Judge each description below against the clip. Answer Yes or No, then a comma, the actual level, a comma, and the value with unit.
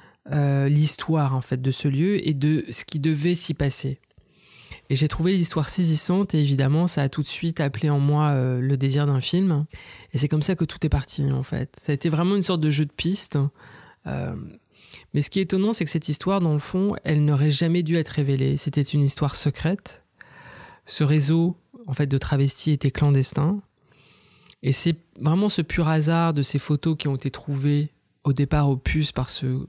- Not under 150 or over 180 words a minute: No, average, 210 wpm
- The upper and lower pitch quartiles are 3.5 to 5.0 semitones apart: No, average, 2.9 semitones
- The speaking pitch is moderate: Yes, medium, 150 Hz